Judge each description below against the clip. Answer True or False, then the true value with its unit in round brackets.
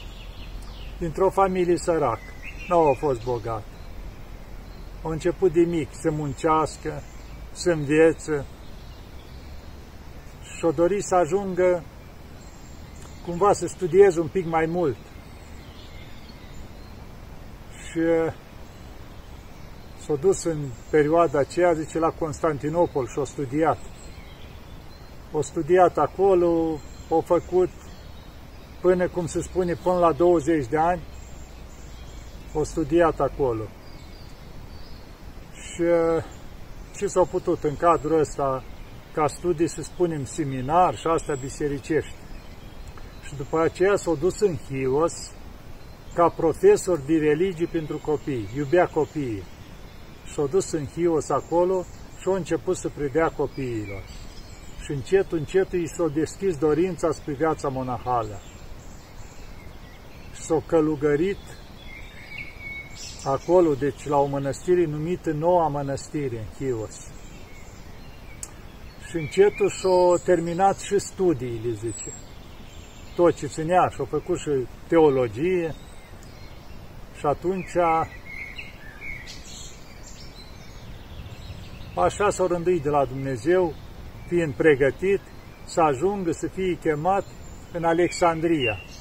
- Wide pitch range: True (7.3 semitones)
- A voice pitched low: False (155 Hz)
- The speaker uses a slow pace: True (105 wpm)